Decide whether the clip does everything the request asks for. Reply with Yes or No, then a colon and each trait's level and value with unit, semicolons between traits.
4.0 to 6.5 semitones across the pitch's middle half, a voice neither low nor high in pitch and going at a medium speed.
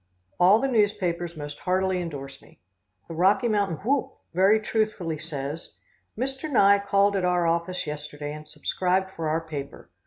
Yes: average, 4.3 semitones; medium, 180 Hz; average, 155 wpm